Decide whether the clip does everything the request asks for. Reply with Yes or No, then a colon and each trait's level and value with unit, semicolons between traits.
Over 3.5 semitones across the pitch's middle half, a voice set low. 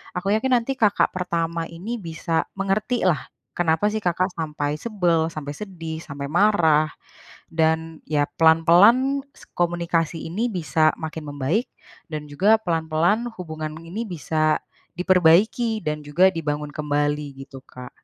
No: average, 4.0 semitones; medium, 165 Hz